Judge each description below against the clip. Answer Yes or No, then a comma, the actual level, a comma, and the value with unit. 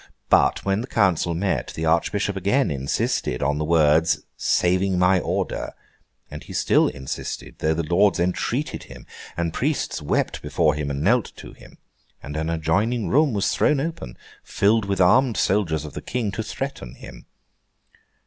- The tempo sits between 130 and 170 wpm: Yes, average, 160 wpm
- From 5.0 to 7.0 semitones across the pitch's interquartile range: Yes, average, 5.3 semitones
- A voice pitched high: No, very low, 90 Hz